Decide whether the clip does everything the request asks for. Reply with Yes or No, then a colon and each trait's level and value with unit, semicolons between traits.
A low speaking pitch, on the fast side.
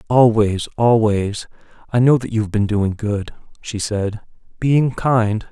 No: low, 110 Hz; average, 140 wpm